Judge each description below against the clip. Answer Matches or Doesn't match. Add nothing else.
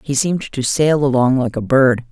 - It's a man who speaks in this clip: Doesn't match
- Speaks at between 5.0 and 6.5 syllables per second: Matches